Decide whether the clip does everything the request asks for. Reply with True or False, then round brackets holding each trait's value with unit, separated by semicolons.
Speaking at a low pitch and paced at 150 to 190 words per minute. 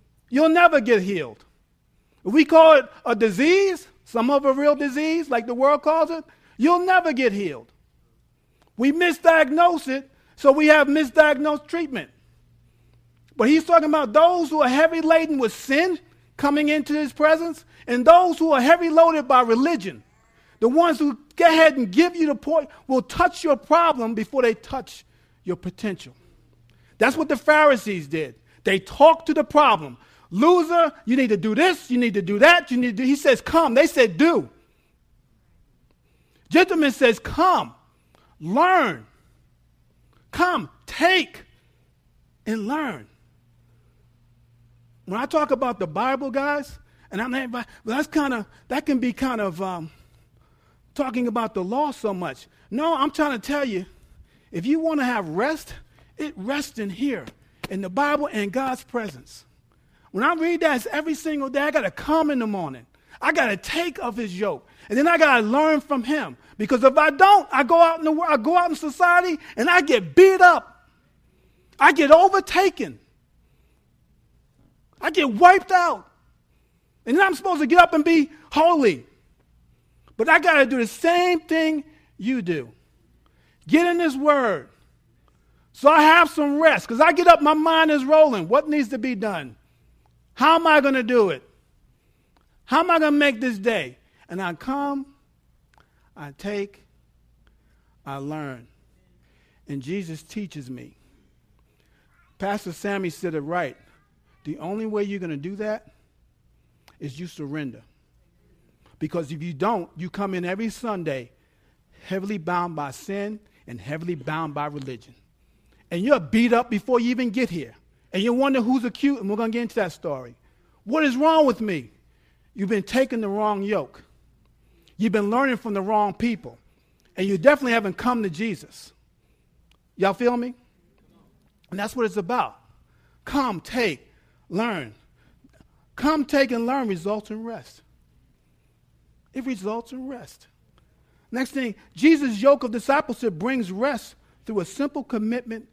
False (255 Hz; 165 wpm)